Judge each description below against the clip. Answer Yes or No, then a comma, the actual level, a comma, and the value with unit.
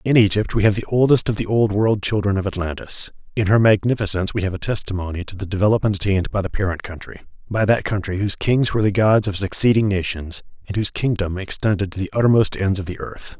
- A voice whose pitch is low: Yes, low, 100 Hz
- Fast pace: Yes, fast, 225 wpm